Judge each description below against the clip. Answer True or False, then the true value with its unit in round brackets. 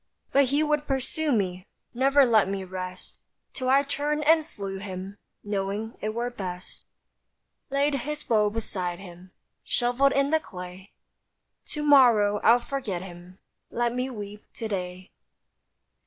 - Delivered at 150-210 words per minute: False (140 wpm)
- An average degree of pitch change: False (6.3 semitones)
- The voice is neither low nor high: False (220 Hz)